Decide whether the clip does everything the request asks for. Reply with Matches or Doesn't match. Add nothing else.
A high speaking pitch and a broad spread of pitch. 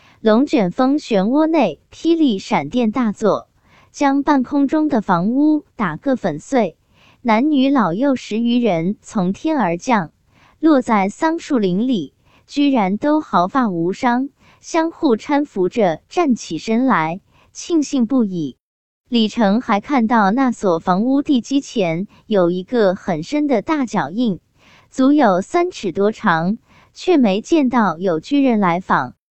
Matches